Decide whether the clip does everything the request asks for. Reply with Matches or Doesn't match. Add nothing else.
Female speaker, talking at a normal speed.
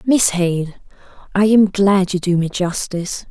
Matches